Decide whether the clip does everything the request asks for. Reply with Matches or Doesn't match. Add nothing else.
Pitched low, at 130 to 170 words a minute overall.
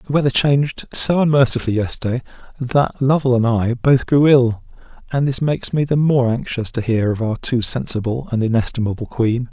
Doesn't match